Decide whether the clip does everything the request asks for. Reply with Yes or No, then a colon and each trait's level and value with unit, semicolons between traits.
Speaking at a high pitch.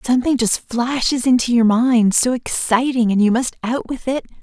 Yes: high, 240 Hz